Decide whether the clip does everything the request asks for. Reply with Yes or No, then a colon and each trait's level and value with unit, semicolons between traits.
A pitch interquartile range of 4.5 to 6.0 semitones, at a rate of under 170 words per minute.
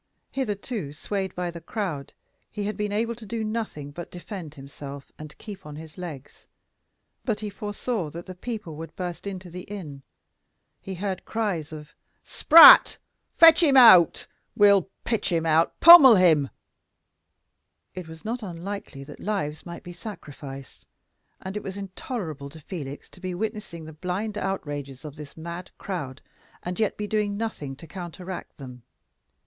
Yes: average, 5.2 semitones; average, 160 wpm